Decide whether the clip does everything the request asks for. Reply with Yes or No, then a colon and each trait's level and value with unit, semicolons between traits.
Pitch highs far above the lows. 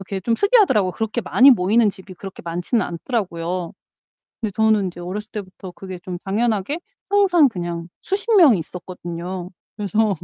No: average, 4.2 semitones